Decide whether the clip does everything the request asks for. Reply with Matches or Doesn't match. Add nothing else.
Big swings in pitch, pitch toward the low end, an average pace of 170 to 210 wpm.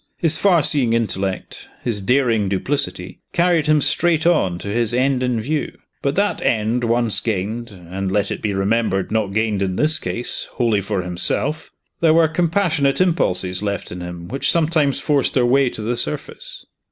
Matches